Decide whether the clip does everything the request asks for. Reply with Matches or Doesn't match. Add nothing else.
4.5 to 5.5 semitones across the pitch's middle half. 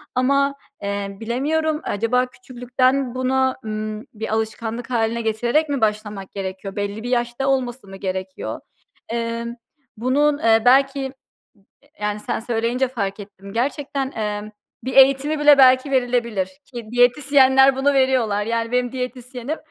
Doesn't match